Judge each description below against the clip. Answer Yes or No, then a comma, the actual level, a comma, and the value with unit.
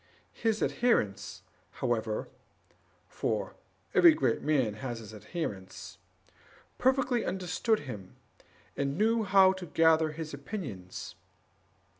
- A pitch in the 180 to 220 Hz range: No, medium, 160 Hz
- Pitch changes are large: Yes, wide, 8.6 semitones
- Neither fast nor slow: No, slow, 100 wpm